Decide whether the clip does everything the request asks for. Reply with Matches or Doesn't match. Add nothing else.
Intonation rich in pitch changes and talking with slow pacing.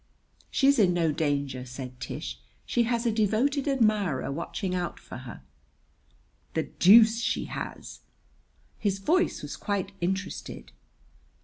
Matches